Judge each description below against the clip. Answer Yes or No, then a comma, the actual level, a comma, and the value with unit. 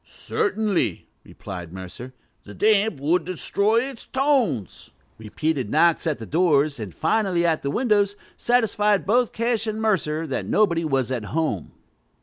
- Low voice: No, medium, 170 Hz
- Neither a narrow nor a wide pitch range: No, wide, 7.8 semitones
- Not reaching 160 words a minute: Yes, average, 140 wpm